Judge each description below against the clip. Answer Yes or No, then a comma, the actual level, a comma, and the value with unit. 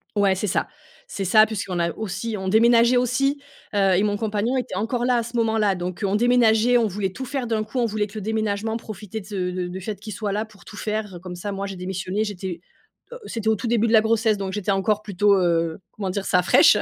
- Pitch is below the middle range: No, high, 210 Hz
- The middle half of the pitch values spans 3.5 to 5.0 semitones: No, average, 2.7 semitones